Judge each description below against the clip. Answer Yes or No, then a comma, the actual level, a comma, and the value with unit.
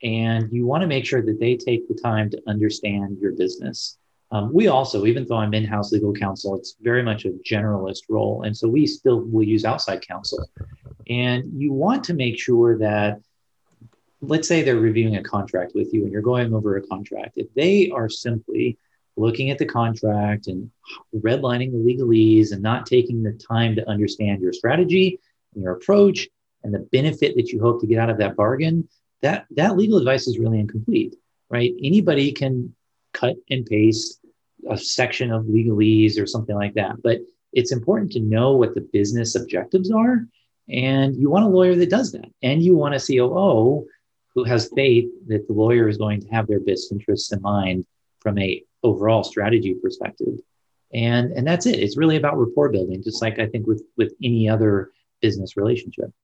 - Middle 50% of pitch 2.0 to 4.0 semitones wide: No, average, 4.5 semitones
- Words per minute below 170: No, average, 190 wpm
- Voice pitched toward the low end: Yes, low, 115 Hz